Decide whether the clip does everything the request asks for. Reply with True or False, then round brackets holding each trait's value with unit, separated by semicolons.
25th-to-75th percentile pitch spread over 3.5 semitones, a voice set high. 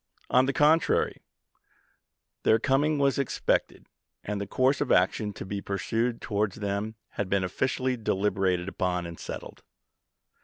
False (5.1 semitones; 105 Hz)